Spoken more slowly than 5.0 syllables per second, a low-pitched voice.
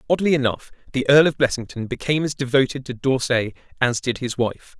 No: 5.9 syllables/s; low, 130 Hz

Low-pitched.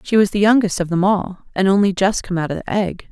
No: high, 190 Hz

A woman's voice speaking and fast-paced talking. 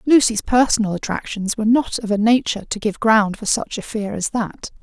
Yes: female; fast, 210 wpm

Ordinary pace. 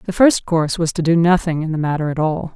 No: fast, 280 wpm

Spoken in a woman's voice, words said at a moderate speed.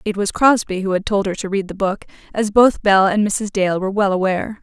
No: female; fast, 260 wpm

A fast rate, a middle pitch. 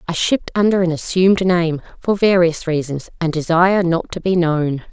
No: average, 185 wpm; medium, 170 Hz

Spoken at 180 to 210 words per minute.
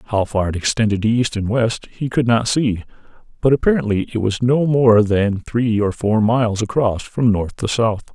Yes: average, 200 wpm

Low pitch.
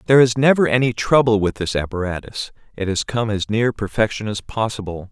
Yes: low, 110 Hz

